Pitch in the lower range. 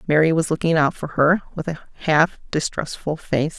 No: medium, 155 Hz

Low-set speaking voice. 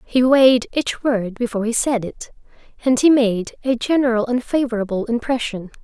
No: high, 240 Hz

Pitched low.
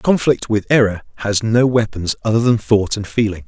Yes: low, 110 Hz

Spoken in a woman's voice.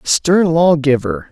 No: male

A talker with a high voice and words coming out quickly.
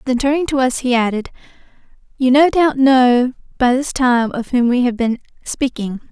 No: very high, 255 Hz; average, 185 wpm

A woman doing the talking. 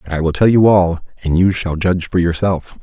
No: male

